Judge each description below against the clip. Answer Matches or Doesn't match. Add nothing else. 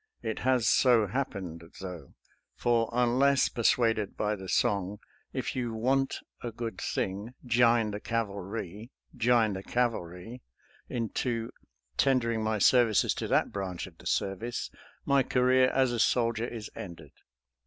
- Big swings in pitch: Doesn't match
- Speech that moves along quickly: Doesn't match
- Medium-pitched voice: Doesn't match